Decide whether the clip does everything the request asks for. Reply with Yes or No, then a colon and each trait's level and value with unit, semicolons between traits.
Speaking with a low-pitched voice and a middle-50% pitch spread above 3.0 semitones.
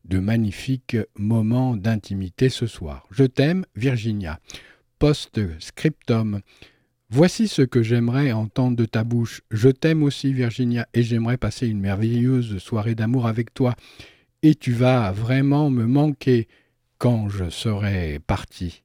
Yes: low, 120 Hz; average, 3.4 semitones